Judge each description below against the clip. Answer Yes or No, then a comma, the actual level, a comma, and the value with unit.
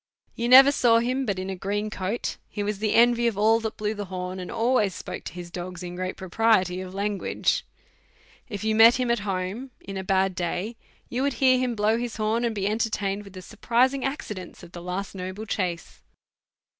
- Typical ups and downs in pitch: Yes, average, 3.8 semitones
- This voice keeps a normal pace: No, fast, 210 wpm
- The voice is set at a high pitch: Yes, high, 210 Hz